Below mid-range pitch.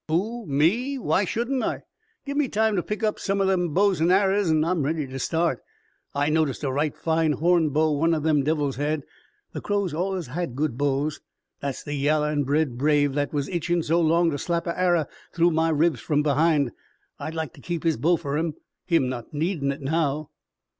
No: medium, 160 Hz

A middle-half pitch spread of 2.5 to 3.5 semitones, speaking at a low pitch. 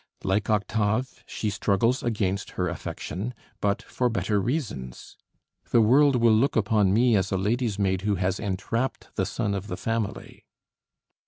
Yes: average, 3.2 semitones; low, 105 Hz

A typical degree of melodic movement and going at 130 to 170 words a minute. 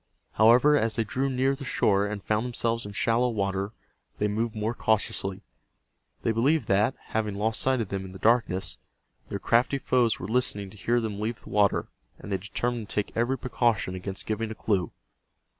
No: average, 3.0 semitones; average, 190 wpm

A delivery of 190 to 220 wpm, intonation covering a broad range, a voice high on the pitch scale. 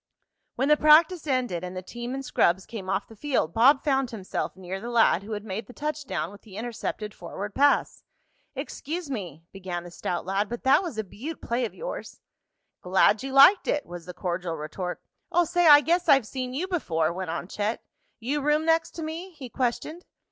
Yes: fast, 205 wpm; wide, 7.8 semitones; high, 240 Hz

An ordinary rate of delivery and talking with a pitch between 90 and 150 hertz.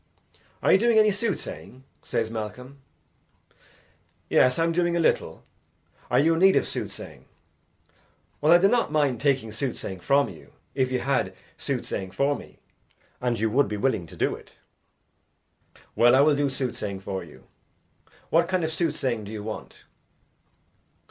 Yes: average, 160 wpm; low, 135 Hz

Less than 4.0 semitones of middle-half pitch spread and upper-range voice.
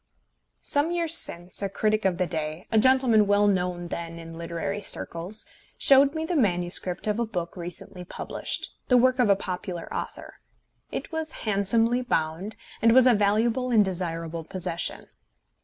No: average, 5.3 semitones; high, 200 Hz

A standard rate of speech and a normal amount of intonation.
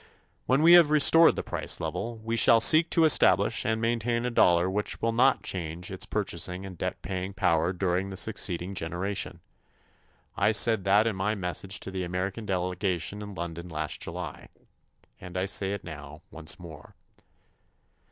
Yes: average, 170 wpm; average, 4.1 semitones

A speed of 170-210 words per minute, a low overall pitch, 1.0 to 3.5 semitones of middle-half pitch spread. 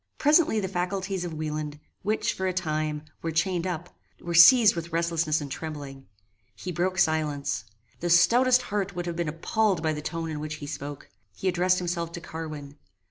No: average, 185 wpm; medium, 170 Hz; average, 3.2 semitones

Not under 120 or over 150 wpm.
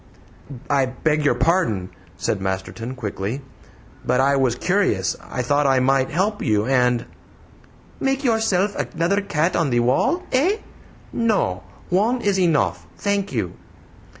Yes: average, 140 wpm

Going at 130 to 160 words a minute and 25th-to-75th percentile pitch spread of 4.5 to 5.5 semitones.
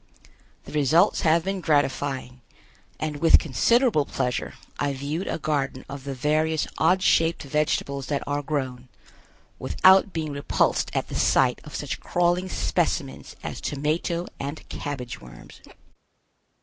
No: slow, 135 wpm; average, 3.2 semitones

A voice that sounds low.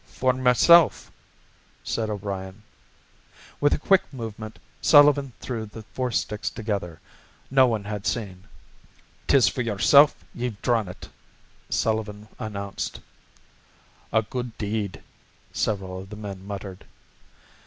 Yes: low, 110 Hz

